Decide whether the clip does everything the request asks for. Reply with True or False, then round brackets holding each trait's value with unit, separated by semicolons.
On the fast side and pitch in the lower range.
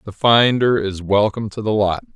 False (195 wpm; 105 Hz)